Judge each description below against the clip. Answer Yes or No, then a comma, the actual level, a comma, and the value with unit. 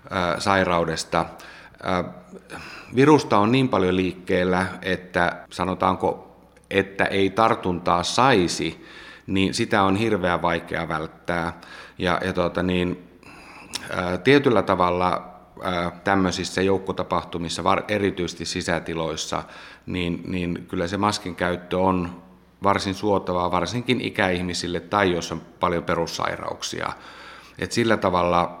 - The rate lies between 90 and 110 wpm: Yes, average, 100 wpm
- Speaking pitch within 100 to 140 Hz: No, very low, 90 Hz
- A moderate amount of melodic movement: No, narrow, 1.9 semitones